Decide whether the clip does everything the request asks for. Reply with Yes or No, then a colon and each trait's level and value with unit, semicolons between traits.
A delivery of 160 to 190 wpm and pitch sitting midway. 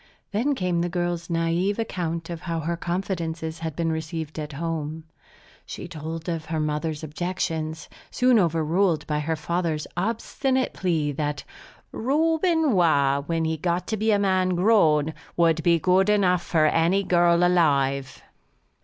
No: average, 150 wpm; medium, 170 Hz